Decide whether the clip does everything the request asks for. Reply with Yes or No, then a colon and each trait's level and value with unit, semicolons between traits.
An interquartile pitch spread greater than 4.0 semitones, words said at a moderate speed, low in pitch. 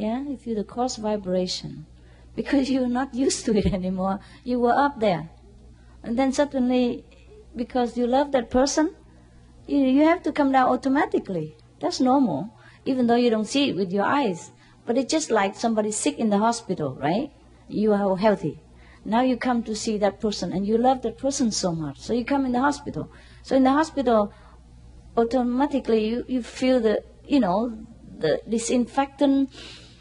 No: average, 4.7 semitones; average, 180 wpm; high, 240 Hz